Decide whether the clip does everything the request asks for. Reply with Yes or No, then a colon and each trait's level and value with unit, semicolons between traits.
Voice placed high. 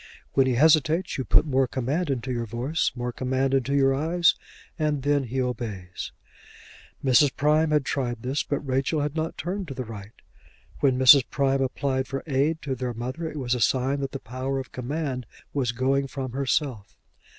No: low, 135 Hz